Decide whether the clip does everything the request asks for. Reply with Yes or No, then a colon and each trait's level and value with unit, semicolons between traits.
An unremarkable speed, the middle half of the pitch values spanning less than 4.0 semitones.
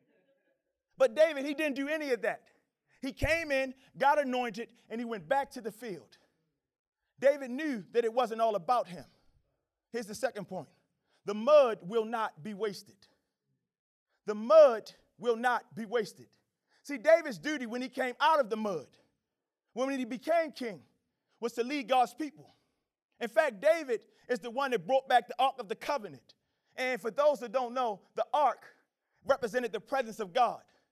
Yes: average, 175 wpm; average, 3.5 semitones